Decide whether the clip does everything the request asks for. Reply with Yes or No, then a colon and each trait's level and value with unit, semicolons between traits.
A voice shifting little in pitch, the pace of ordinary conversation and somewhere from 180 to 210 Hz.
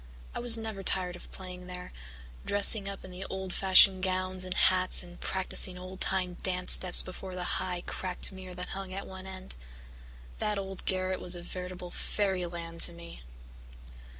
Yes: narrow, 0.9 semitones; average, 175 wpm; medium, 185 Hz